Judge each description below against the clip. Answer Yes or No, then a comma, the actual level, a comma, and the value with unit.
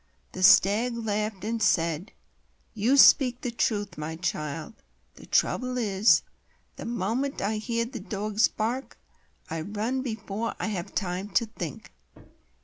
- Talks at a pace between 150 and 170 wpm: No, slow, 135 wpm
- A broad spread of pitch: No, average, 3.5 semitones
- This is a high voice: Yes, high, 215 Hz